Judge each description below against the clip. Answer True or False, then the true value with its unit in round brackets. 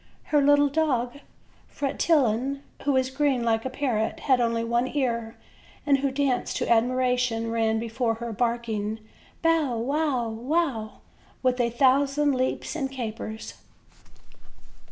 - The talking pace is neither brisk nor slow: False (130 wpm)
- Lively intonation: False (3.3 semitones)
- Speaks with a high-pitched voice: True (250 Hz)